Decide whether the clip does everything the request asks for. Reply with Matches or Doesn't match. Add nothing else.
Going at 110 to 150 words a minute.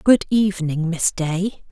Matches